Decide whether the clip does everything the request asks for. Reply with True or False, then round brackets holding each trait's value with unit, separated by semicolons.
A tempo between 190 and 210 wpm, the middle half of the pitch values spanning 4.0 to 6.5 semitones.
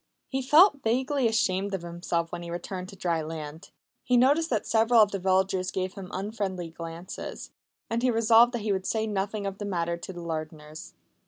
True (195 wpm; 4.7 semitones)